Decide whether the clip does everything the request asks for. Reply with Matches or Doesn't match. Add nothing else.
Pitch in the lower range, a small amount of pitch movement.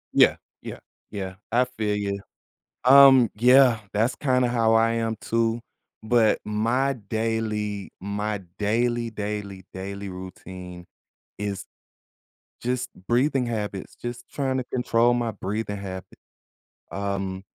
Doesn't match